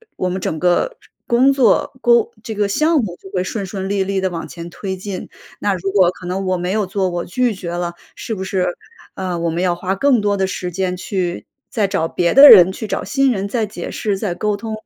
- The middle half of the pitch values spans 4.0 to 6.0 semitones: No, average, 2.8 semitones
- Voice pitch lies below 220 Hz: Yes, high, 190 Hz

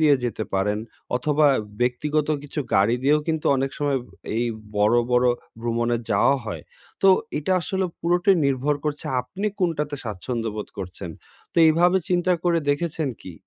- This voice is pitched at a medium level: Yes, medium, 145 Hz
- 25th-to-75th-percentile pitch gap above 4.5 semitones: Yes, average, 5.3 semitones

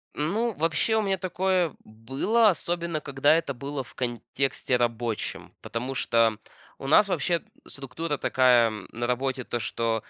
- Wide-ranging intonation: Yes, wide, 6.0 semitones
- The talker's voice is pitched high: No, low, 135 Hz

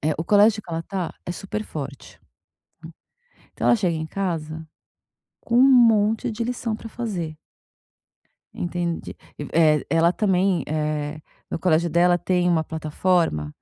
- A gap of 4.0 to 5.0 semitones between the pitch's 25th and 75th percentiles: Yes, average, 4.6 semitones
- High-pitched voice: No, medium, 175 Hz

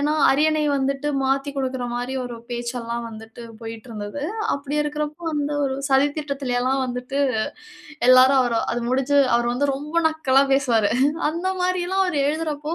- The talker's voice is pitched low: No, very high, 270 Hz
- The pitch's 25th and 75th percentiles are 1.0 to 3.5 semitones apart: Yes, average, 3.2 semitones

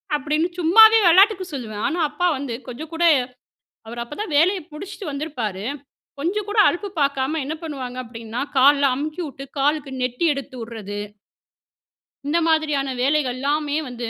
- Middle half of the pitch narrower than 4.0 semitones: No, average, 4.3 semitones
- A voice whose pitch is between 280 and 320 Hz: Yes, very high, 290 Hz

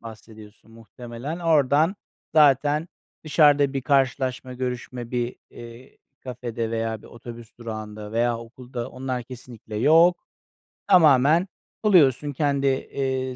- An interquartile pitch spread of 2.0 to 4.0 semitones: Yes, average, 3.5 semitones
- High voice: No, low, 130 Hz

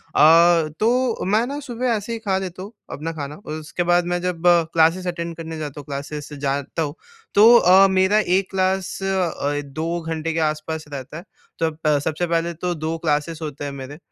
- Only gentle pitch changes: No, average, 3.6 semitones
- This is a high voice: No, medium, 165 Hz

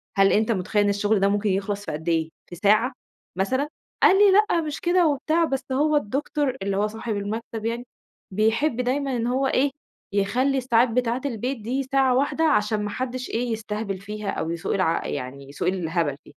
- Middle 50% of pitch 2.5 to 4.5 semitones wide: No, average, 4.9 semitones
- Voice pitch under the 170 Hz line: No, high, 225 Hz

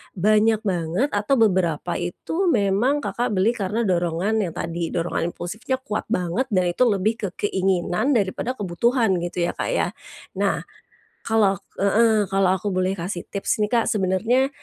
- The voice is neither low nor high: No, high, 200 Hz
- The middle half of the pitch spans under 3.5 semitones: No, average, 3.9 semitones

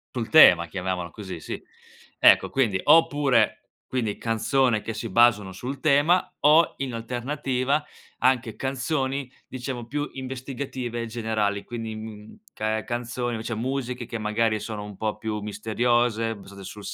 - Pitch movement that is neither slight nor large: Yes, average, 3.5 semitones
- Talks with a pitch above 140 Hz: No, low, 115 Hz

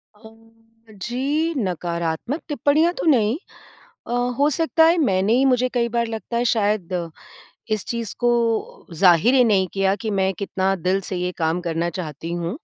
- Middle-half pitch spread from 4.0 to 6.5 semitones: Yes, average, 5.2 semitones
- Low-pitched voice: No, high, 215 Hz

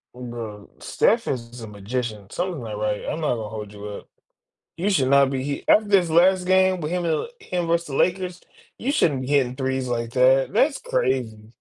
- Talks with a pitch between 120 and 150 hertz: Yes, low, 135 Hz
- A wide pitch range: Yes, wide, 7.2 semitones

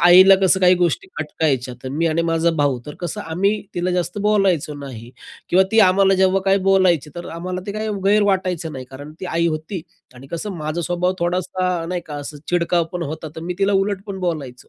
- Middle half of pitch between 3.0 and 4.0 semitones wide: Yes, average, 3.4 semitones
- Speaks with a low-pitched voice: No, medium, 175 Hz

